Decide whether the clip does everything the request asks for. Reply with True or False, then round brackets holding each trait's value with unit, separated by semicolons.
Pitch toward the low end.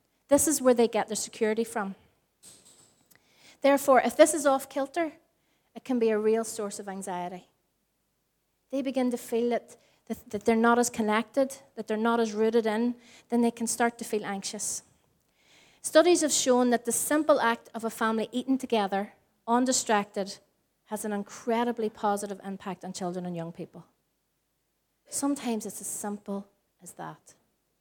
False (230 Hz)